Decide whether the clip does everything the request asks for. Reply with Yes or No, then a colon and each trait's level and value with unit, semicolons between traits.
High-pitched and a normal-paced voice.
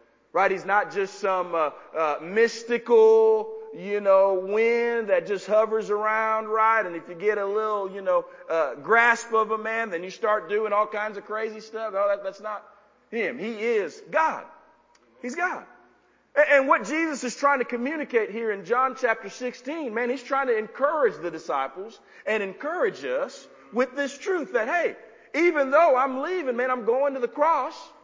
Yes: high, 230 Hz; average, 185 wpm